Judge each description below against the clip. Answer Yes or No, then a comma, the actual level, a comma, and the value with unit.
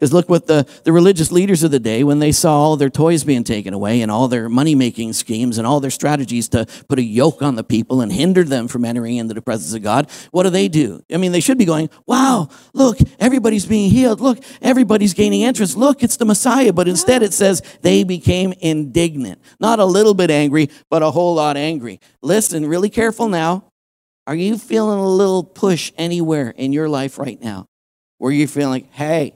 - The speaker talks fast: Yes, fast, 215 wpm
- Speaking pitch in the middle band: Yes, medium, 160 Hz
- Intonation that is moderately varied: No, wide, 6.8 semitones